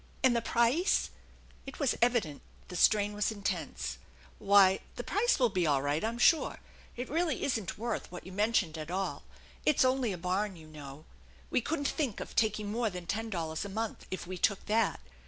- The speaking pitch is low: No, high, 210 Hz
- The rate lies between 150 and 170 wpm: No, average, 200 wpm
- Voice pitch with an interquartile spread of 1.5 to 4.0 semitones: No, average, 4.8 semitones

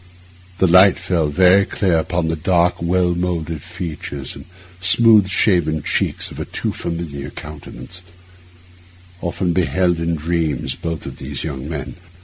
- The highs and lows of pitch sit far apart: No, average, 2.8 semitones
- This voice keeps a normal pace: Yes, average, 145 wpm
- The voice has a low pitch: Yes, very low, 85 Hz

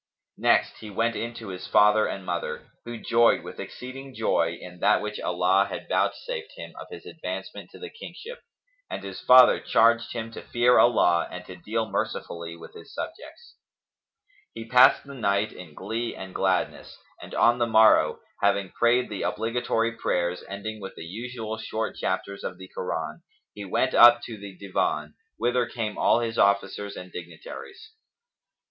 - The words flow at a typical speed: Yes, average, 170 wpm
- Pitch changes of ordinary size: Yes, average, 3.9 semitones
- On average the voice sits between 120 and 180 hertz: No, low, 110 Hz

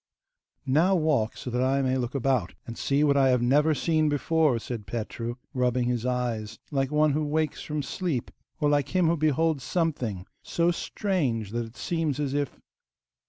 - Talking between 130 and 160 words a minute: No, average, 180 wpm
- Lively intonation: No, average, 4.2 semitones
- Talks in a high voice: No, medium, 140 Hz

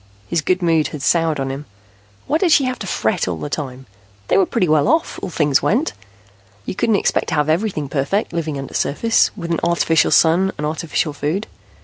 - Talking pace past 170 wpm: Yes, fast, 205 wpm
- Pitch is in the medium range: Yes, medium, 165 Hz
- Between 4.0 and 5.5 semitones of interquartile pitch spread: Yes, average, 4.5 semitones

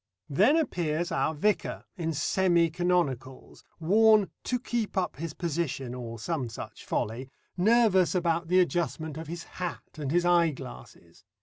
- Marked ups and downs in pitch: No, average, 3.6 semitones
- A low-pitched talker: No, medium, 170 Hz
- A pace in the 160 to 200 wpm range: No, average, 140 wpm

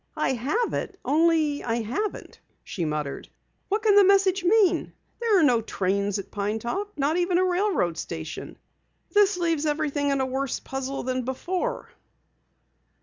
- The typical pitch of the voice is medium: No, very high, 295 Hz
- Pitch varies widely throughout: Yes, wide, 8.0 semitones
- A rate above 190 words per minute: No, average, 155 wpm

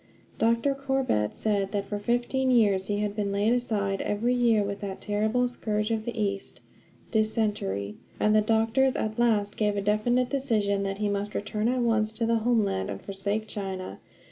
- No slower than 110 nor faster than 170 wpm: No, average, 180 wpm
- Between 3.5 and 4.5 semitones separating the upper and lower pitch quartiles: No, narrow, 2.6 semitones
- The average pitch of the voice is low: No, high, 215 Hz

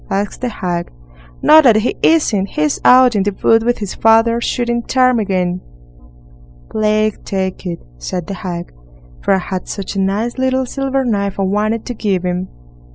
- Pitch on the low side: No, high, 215 Hz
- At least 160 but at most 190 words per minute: Yes, average, 170 wpm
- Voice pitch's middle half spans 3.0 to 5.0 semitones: Yes, average, 4.1 semitones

